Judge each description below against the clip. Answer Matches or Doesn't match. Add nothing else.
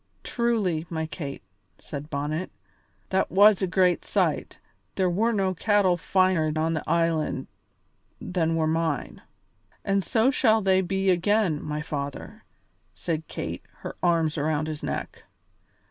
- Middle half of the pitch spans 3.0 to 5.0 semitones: Matches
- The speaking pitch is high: Doesn't match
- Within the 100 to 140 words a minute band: Matches